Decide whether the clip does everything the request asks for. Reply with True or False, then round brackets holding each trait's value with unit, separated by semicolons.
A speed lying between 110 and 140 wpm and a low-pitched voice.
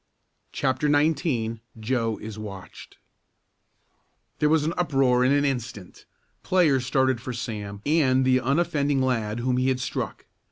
True (135 wpm; 130 Hz)